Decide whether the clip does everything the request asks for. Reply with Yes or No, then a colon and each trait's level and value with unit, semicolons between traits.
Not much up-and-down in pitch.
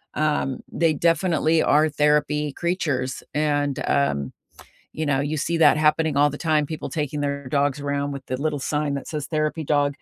Yes: narrow, 1.5 semitones